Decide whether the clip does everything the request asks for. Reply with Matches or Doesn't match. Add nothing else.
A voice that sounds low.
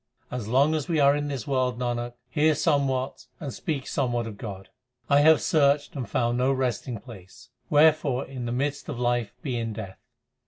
Matches